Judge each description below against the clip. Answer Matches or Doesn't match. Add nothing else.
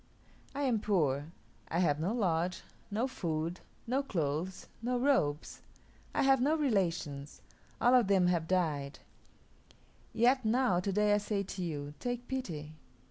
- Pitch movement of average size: Doesn't match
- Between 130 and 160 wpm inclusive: Matches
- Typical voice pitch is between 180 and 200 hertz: Matches